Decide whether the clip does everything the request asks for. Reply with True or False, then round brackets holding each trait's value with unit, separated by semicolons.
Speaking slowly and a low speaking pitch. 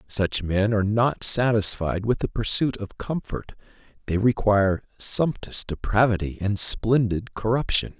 True (130 wpm; 105 Hz)